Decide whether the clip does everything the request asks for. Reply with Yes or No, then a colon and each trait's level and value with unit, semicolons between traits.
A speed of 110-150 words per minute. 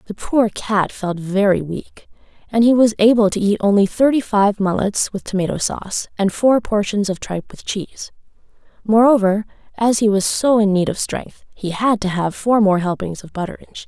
No: average, 200 wpm